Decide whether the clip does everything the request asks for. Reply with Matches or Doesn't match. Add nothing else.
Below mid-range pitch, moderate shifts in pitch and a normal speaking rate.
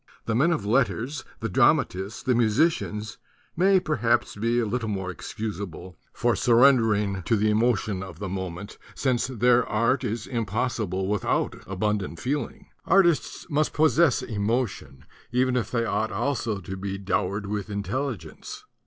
Matches